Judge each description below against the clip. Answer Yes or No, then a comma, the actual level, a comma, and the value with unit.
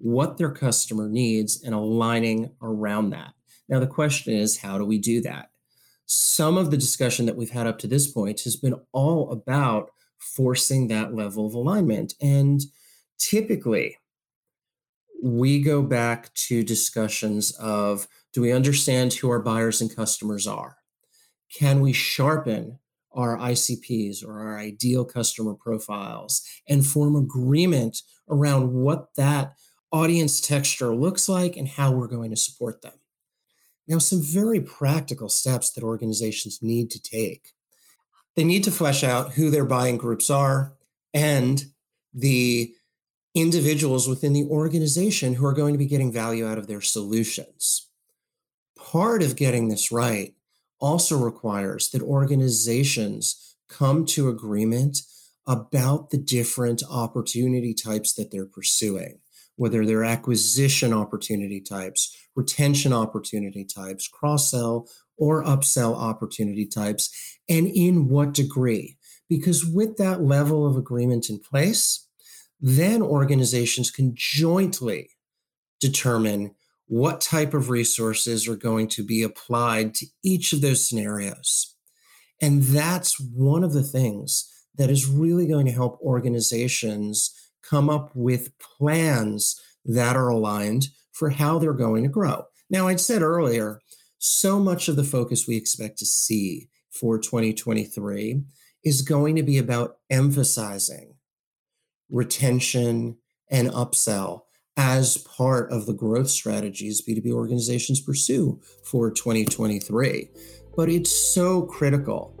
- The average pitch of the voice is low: Yes, low, 125 Hz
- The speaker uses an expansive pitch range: No, average, 4.3 semitones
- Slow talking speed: Yes, slow, 130 wpm